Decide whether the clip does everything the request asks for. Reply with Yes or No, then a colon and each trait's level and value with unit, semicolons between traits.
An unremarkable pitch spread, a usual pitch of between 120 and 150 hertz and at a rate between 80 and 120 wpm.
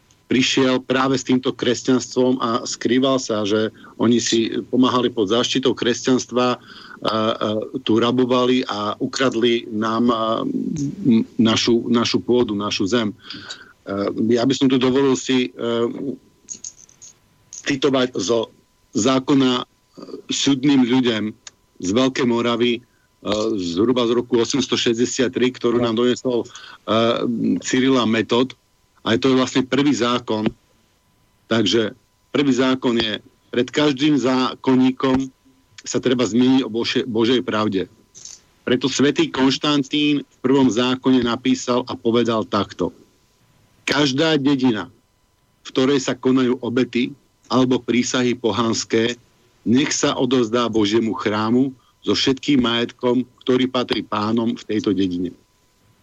No: narrow, 2.3 semitones; low, 125 Hz; average, 115 wpm